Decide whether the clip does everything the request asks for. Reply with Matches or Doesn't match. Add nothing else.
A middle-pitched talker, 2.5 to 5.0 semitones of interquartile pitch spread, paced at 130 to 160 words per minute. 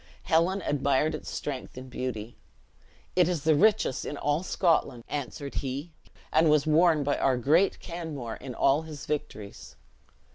Matches